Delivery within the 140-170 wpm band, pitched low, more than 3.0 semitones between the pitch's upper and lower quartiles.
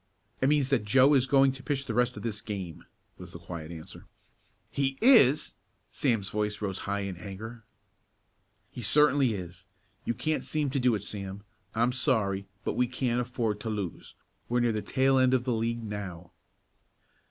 No: average, 180 wpm; low, 115 Hz; average, 4.7 semitones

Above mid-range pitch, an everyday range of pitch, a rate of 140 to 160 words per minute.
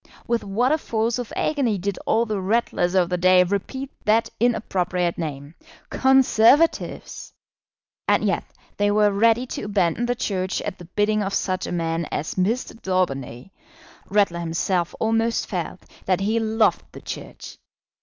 Yes: high, 205 Hz; average, 4.1 semitones; average, 155 wpm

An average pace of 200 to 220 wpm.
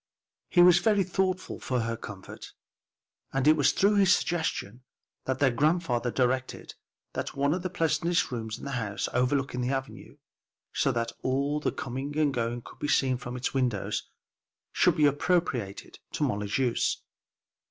No: average, 165 wpm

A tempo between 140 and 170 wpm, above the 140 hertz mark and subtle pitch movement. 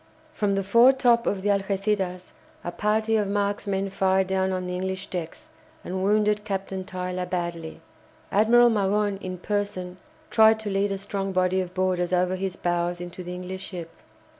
Yes: average, 165 wpm; high, 190 Hz; narrow, 2.1 semitones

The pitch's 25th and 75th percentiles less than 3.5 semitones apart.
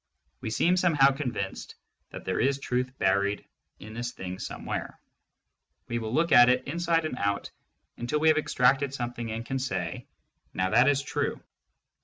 No: average, 4.2 semitones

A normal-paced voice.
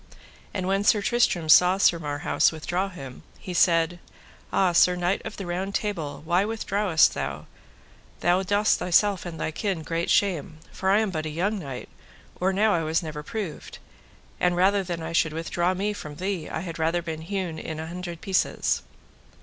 Yes: average, 190 wpm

